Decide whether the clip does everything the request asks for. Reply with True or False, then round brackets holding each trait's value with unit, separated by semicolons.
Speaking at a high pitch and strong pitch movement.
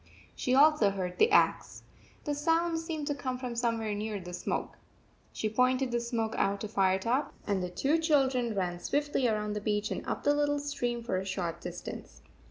True (235 Hz; 6.1 semitones)